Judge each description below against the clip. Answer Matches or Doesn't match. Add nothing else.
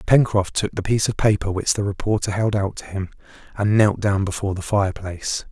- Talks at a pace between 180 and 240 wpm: Matches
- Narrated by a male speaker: Matches